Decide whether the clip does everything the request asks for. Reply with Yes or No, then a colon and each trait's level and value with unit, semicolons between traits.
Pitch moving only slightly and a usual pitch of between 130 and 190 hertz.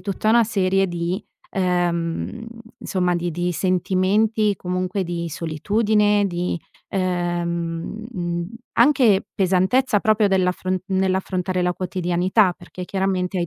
Yes: narrow, 2.3 semitones; medium, 185 Hz